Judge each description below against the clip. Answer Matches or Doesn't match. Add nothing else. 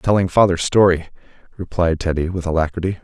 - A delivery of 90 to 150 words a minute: Matches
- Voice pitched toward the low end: Matches